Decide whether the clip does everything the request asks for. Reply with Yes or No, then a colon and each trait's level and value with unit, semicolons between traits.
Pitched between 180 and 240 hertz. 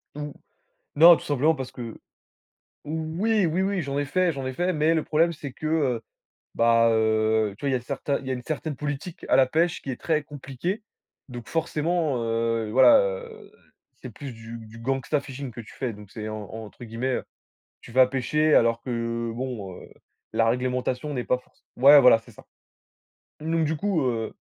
No: low, 130 Hz